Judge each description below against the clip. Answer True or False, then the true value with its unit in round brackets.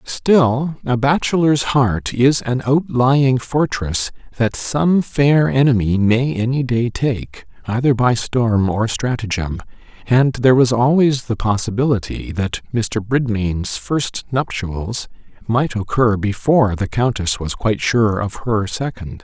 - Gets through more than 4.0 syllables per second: False (3.8 syllables/s)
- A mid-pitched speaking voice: False (120 Hz)